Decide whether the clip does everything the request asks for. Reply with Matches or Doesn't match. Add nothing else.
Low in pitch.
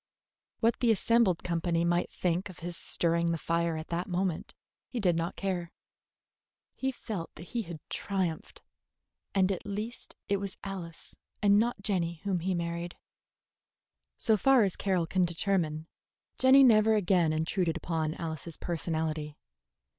Doesn't match